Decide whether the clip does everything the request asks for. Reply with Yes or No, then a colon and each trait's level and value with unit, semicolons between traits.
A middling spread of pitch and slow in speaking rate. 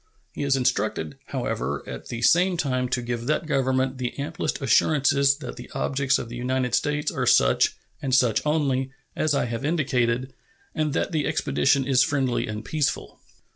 No: average, 3.0 semitones; average, 175 wpm